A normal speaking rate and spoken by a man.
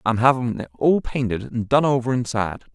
Yes: average, 195 wpm; male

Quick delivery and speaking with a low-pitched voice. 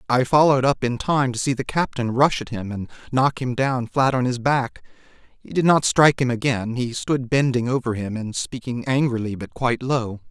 Yes: fast, 215 wpm; low, 125 Hz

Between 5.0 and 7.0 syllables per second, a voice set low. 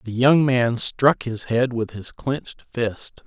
No: 3.5 syllables/s; low, 120 Hz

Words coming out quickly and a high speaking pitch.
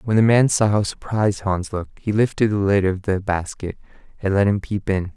No: fast, 235 wpm; low, 100 Hz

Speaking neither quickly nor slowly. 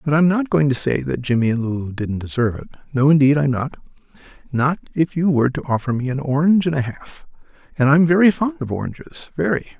No: fast, 220 wpm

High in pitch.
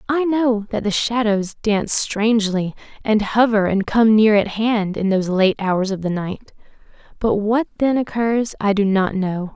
Yes: high, 210 Hz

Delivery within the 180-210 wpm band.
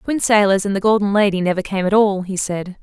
No: fast, 275 wpm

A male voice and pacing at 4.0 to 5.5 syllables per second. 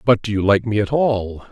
Yes: male; 5.0 syllables/s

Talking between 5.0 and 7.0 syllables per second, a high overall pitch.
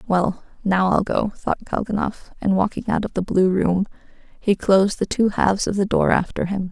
Yes: 5.1 syllables/s; high, 195 Hz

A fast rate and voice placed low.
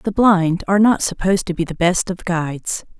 No: fast, 220 wpm; medium, 185 Hz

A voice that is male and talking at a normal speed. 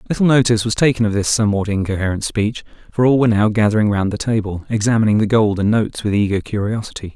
No: male; fast, 210 wpm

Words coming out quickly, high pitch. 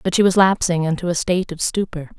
No: fast, 245 wpm; medium, 175 Hz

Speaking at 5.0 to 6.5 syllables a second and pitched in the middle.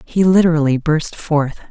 No: 4.7 syllables/s; medium, 160 Hz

